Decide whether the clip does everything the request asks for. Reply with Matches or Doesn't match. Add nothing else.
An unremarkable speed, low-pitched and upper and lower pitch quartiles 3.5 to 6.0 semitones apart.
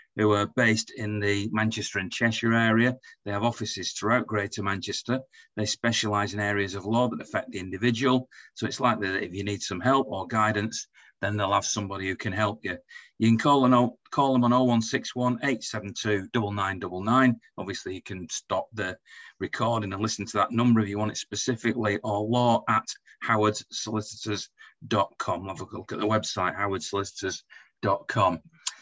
Doesn't match